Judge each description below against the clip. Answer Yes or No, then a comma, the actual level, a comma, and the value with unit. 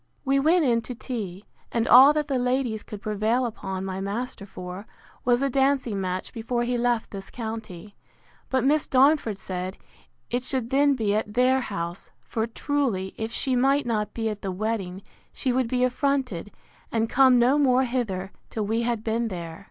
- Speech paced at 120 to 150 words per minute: No, average, 185 wpm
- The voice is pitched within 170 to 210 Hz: No, high, 235 Hz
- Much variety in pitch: No, average, 4.2 semitones